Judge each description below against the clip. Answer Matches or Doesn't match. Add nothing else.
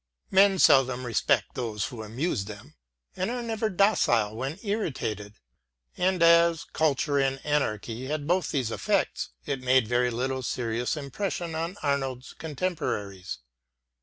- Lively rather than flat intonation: Matches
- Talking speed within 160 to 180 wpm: Doesn't match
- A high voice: Doesn't match